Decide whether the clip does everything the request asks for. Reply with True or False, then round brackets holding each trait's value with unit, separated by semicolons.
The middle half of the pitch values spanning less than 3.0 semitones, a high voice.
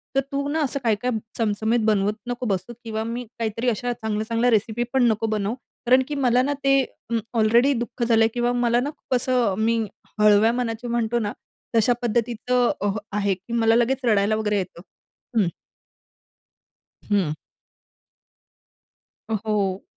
True (2.4 semitones; 230 Hz)